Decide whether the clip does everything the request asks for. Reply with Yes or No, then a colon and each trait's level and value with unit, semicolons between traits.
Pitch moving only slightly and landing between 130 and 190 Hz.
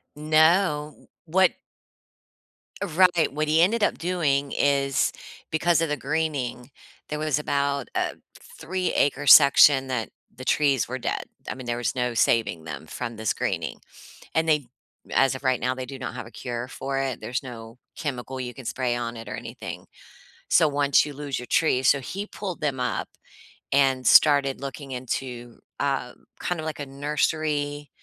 No: average, 3.2 semitones; medium, 140 Hz